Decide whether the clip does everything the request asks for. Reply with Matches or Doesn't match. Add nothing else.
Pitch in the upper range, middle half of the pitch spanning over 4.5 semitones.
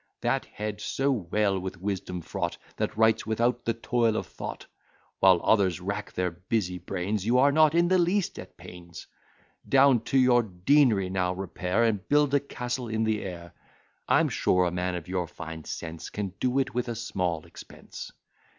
Doesn't match